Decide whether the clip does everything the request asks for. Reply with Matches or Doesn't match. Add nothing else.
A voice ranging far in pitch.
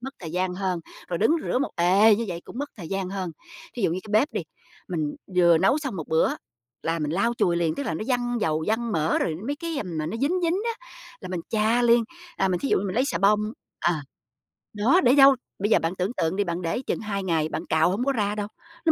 Matches